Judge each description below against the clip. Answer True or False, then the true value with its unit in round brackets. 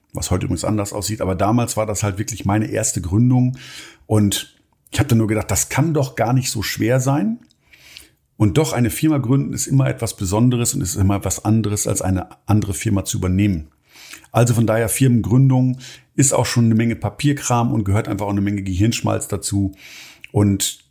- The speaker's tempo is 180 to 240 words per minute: True (190 wpm)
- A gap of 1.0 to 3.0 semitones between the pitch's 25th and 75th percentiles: False (3.6 semitones)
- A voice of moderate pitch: False (110 Hz)